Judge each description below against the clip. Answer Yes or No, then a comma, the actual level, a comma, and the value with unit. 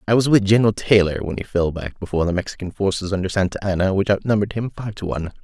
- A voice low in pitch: Yes, low, 100 Hz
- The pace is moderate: No, fast, 245 wpm